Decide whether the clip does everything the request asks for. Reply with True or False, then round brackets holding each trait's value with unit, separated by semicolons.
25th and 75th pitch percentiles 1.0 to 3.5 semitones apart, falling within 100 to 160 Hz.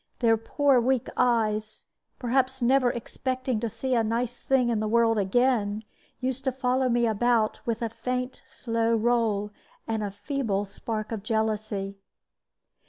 False (2.7 semitones; 230 Hz)